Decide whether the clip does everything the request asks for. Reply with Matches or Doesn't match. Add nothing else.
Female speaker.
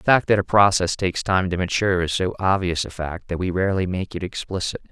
Doesn't match